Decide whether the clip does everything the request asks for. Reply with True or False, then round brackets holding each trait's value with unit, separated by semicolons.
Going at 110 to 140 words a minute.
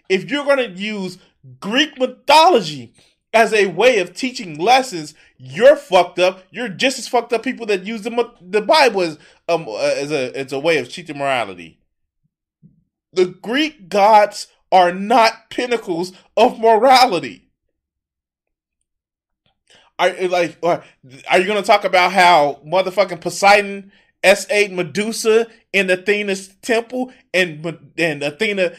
True (135 wpm)